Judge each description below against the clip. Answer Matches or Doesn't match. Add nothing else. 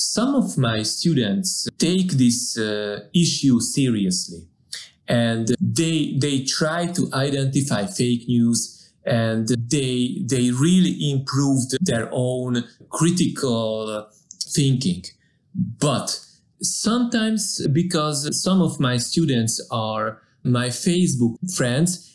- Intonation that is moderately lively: Doesn't match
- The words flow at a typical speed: Doesn't match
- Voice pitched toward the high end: Doesn't match